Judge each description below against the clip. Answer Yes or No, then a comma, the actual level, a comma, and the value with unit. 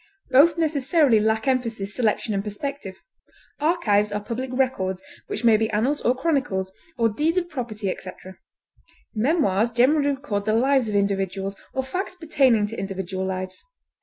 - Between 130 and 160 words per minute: Yes, average, 150 wpm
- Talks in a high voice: Yes, high, 230 Hz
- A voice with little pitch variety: No, wide, 5.5 semitones